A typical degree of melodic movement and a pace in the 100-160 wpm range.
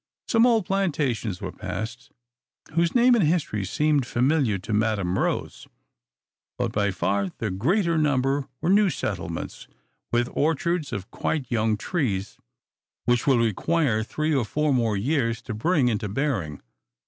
No: wide, 6.7 semitones; average, 150 wpm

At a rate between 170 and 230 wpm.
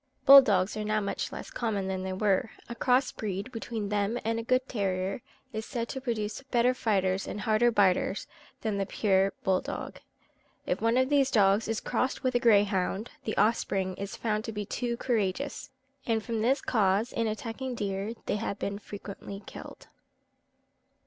Yes: average, 180 wpm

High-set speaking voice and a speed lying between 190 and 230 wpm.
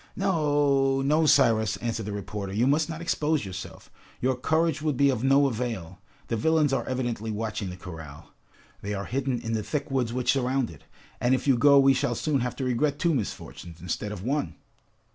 No: low, 125 Hz; average, 200 wpm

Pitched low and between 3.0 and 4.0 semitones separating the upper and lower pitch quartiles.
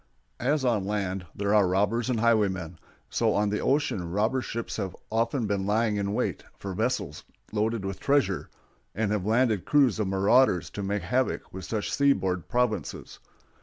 Yes: low, 105 Hz; average, 3.4 semitones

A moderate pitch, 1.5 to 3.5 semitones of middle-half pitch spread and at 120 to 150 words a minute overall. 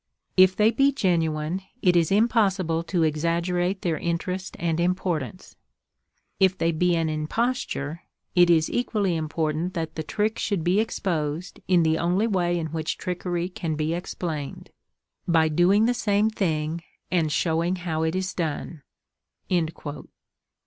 Yes: medium, 175 Hz; average, 2.8 semitones; average, 140 wpm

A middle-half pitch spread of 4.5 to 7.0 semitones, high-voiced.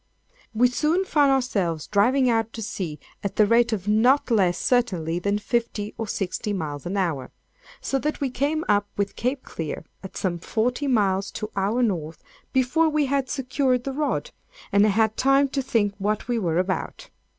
Yes: average, 5.1 semitones; high, 225 Hz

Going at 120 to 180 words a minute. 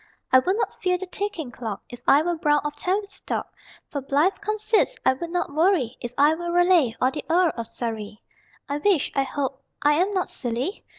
No: average, 200 wpm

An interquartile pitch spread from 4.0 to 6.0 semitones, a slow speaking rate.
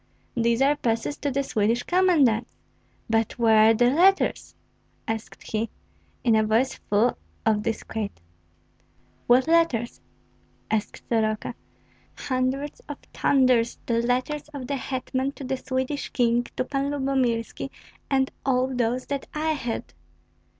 No: average, 3.2 semitones; slow, 130 wpm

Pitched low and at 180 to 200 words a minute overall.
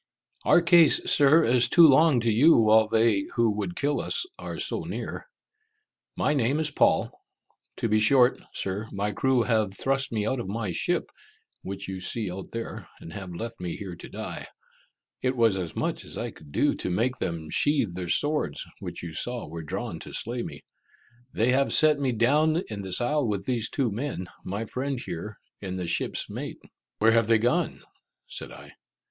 Yes: low, 115 Hz; average, 190 wpm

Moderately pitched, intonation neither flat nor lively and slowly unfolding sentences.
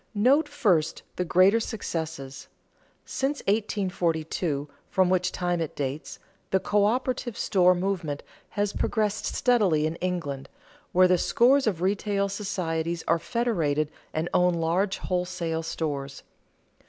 Yes: medium, 180 Hz; average, 4.1 semitones; slow, 125 wpm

